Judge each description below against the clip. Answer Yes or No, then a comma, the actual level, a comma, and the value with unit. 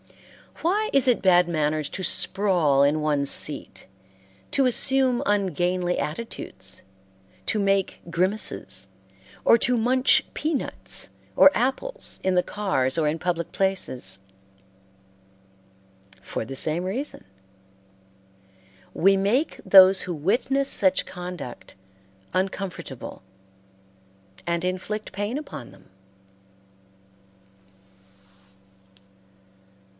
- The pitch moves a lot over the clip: Yes, wide, 6.3 semitones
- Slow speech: Yes, slow, 95 wpm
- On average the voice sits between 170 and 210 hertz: Yes, medium, 185 Hz